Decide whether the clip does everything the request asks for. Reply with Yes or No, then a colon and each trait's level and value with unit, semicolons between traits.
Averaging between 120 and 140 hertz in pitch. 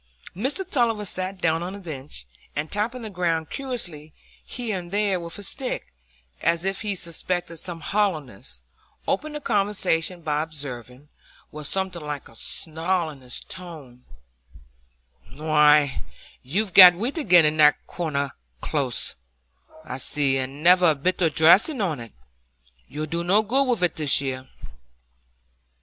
No: medium, 170 Hz